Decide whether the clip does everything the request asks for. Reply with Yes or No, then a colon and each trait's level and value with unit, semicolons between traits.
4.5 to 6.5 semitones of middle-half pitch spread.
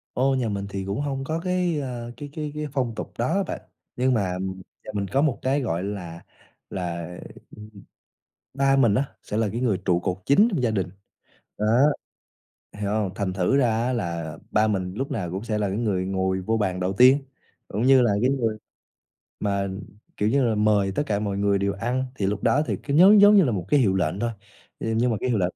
Yes: average, 5.3 semitones